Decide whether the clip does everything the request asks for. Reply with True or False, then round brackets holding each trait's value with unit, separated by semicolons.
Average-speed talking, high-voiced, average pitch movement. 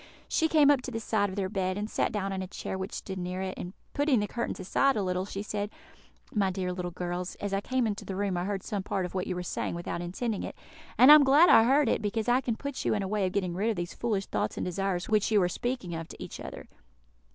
False (285 wpm; 200 Hz; 3.6 semitones)